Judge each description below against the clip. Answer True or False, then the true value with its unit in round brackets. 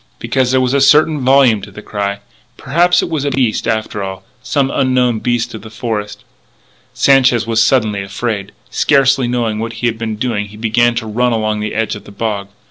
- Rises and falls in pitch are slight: False (3.4 semitones)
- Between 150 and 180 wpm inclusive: False (200 wpm)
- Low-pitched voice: True (115 Hz)